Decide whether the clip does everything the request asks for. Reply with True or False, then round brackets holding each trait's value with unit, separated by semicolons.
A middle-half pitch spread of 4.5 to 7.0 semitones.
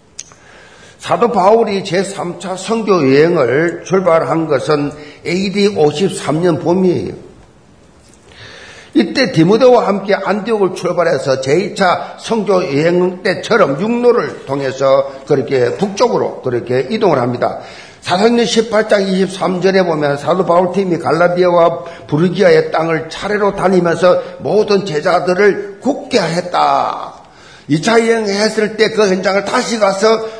False (3.8 semitones)